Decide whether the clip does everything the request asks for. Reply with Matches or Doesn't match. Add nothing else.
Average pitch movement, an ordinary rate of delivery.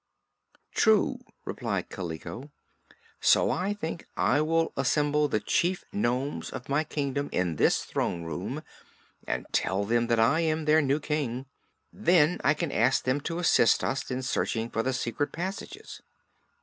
Matches